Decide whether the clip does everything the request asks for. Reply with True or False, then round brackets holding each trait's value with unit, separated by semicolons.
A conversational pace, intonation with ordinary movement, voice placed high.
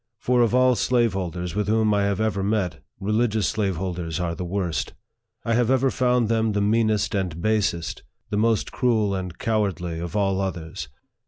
False (170 wpm; 3.6 semitones; 105 Hz)